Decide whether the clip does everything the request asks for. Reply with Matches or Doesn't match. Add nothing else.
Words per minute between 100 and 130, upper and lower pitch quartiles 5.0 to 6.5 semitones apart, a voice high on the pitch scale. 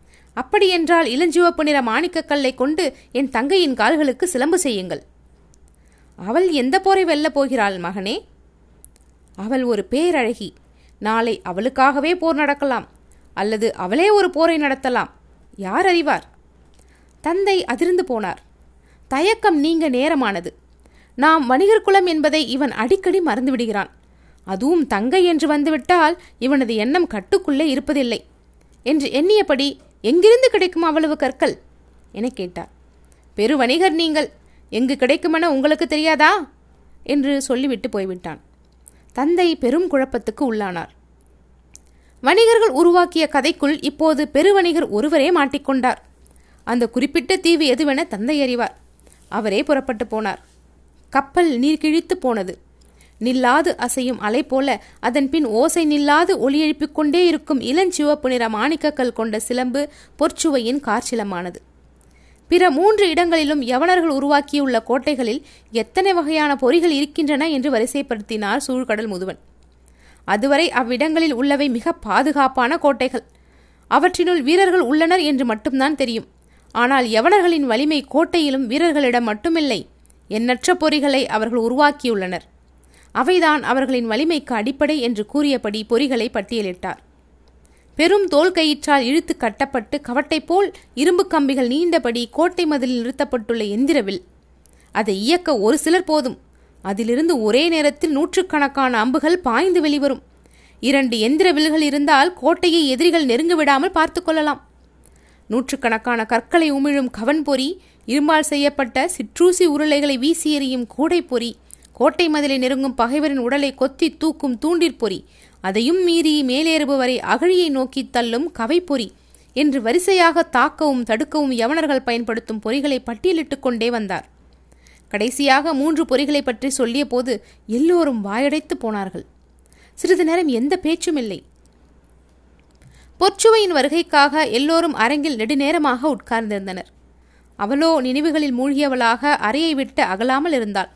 Matches